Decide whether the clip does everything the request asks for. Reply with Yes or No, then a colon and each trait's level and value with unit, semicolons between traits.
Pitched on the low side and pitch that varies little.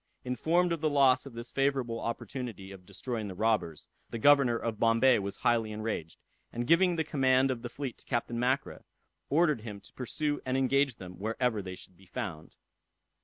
No: low, 120 Hz; average, 4.1 semitones